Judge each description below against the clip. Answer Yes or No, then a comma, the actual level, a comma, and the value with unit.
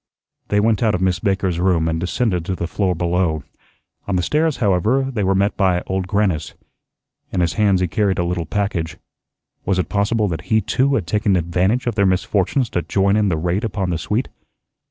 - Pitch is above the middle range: No, very low, 95 Hz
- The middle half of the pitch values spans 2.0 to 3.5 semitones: Yes, average, 3.0 semitones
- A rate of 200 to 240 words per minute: Yes, fast, 205 wpm